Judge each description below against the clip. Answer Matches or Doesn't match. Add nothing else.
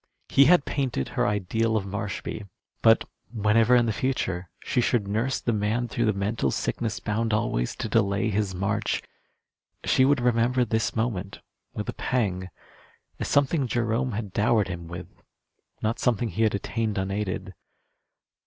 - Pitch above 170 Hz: Doesn't match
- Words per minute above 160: Doesn't match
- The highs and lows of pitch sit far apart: Doesn't match